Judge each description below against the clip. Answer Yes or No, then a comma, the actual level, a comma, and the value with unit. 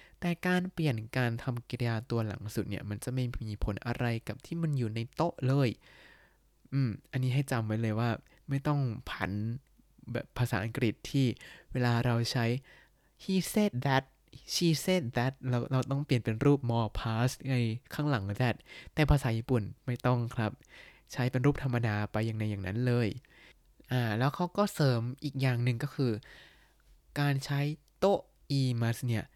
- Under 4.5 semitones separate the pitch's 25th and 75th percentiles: Yes, average, 3.4 semitones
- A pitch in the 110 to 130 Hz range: Yes, low, 125 Hz